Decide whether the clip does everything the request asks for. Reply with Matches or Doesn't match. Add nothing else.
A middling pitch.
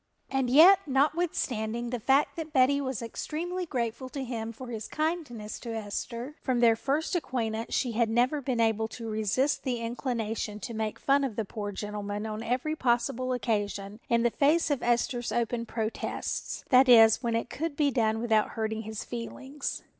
Doesn't match